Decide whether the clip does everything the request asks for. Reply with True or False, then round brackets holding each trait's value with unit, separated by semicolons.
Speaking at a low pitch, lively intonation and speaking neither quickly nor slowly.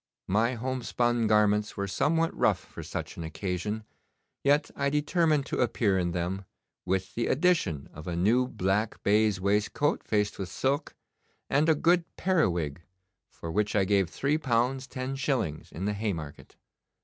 True (105 Hz; 6.2 semitones; 155 wpm)